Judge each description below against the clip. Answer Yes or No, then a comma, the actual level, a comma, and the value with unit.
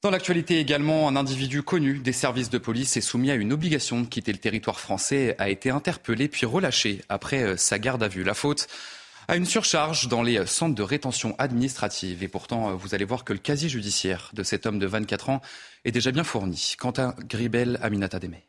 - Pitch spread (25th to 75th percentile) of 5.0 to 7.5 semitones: Yes, wide, 5.6 semitones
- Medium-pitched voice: No, low, 120 Hz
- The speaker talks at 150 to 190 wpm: No, average, 210 wpm